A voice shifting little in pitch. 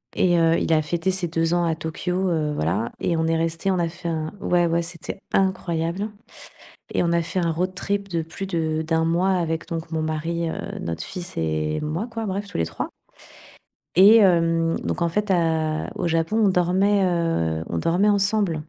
Yes: narrow, 2.3 semitones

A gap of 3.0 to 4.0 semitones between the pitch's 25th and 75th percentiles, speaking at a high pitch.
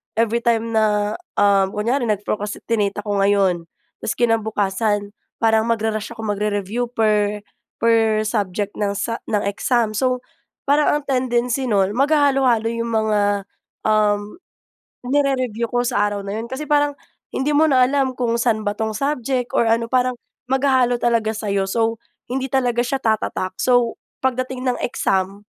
Yes: average, 3.3 semitones; high, 225 Hz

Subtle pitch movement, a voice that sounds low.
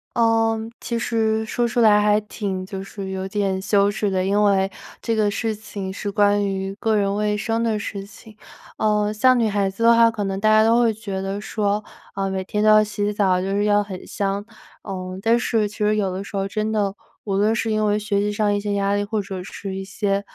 No: narrow, 1.7 semitones; high, 205 Hz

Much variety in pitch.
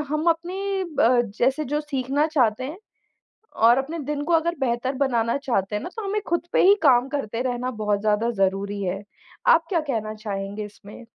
Yes: wide, 6.1 semitones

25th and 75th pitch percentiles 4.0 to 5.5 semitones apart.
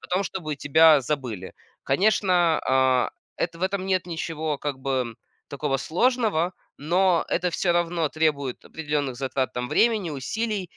Yes: average, 4.9 semitones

